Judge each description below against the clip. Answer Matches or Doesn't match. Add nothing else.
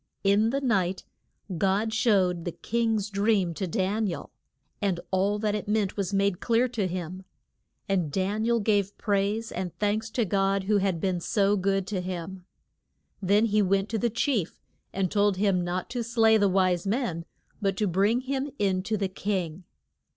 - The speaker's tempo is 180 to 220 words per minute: Matches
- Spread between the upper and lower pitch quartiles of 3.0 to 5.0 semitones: Doesn't match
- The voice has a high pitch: Matches